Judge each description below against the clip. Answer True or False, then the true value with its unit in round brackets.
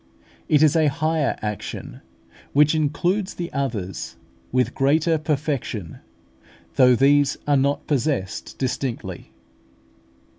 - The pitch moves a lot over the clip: False (3.3 semitones)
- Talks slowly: True (105 wpm)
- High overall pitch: False (140 Hz)